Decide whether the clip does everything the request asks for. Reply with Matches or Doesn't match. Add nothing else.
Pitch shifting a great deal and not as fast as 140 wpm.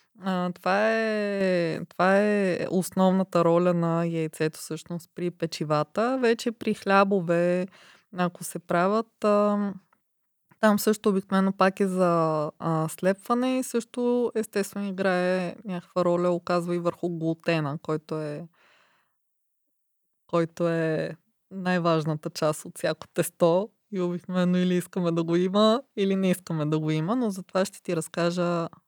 Doesn't match